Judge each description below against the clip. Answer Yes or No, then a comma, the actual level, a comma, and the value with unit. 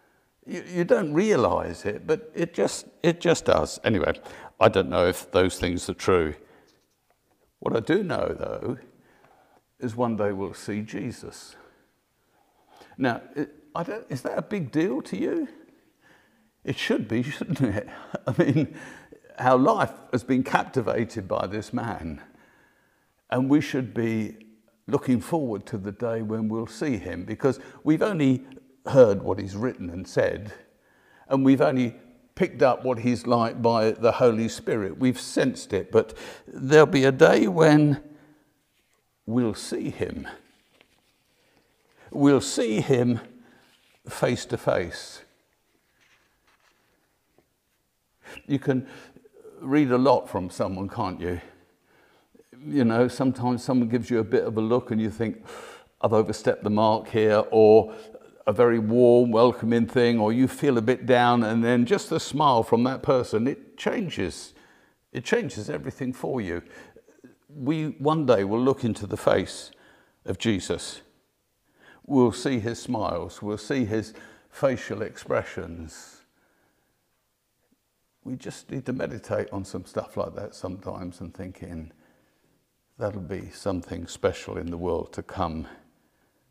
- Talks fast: No, average, 145 wpm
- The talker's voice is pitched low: Yes, low, 120 Hz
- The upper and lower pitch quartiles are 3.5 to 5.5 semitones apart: Yes, average, 4.1 semitones